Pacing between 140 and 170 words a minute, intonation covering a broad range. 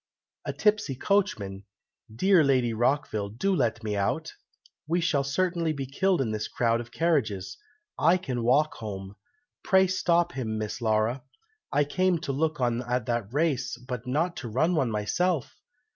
Yes: average, 160 wpm; wide, 6.9 semitones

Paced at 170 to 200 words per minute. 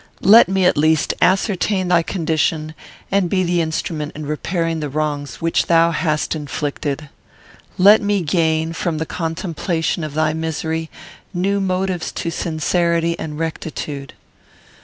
No: slow, 135 wpm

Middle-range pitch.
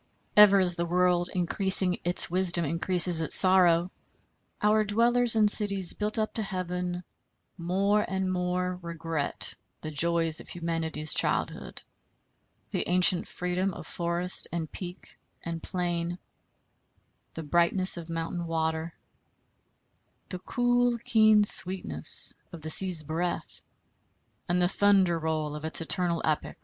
Yes: medium, 180 Hz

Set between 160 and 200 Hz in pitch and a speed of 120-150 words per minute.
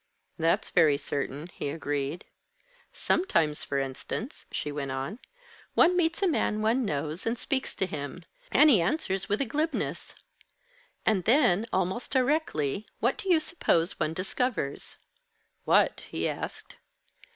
Yes: high, 190 Hz; average, 140 wpm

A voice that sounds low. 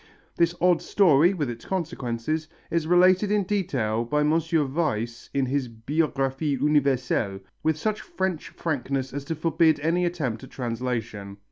No: medium, 150 Hz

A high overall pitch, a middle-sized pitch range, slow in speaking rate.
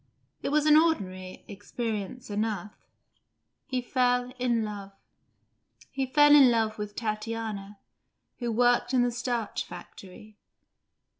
Yes: high, 230 Hz; average, 3.2 semitones; slow, 120 wpm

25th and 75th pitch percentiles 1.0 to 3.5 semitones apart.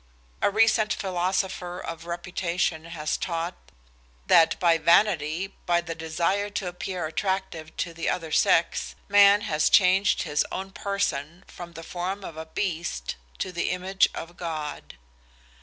Yes: narrow, 2.6 semitones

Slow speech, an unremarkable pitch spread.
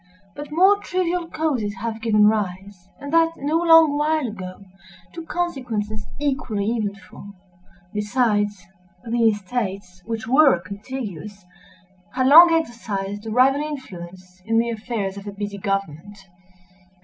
No: slow, 120 wpm; wide, 6.1 semitones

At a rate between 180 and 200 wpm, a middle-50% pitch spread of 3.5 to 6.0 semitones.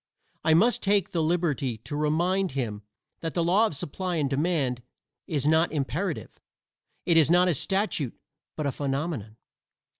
No: average, 155 wpm; average, 4.3 semitones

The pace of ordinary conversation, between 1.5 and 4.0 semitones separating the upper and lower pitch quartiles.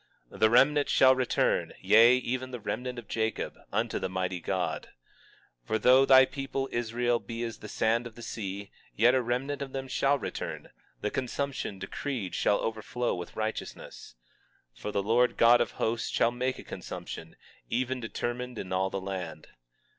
Yes: average, 175 wpm; average, 3.4 semitones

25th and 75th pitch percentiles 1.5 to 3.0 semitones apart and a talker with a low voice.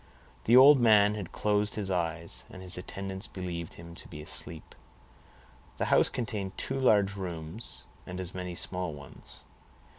No: average, 3.5 semitones; very low, 95 Hz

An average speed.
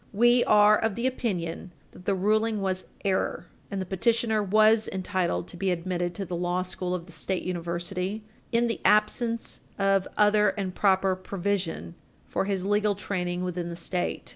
Yes: average, 170 wpm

